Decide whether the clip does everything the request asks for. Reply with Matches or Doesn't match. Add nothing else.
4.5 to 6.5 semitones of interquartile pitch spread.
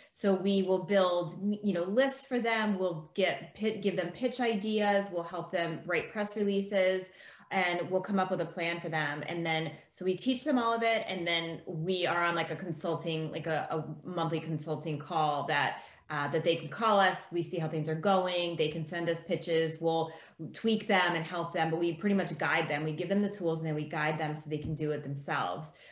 Doesn't match